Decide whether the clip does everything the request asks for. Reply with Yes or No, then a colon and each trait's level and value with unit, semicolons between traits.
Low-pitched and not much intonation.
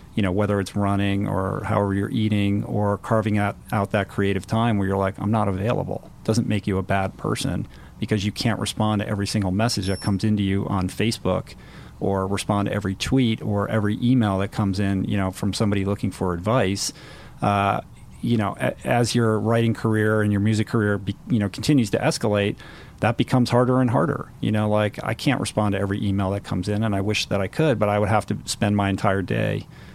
Yes: low, 105 Hz; narrow, 1.9 semitones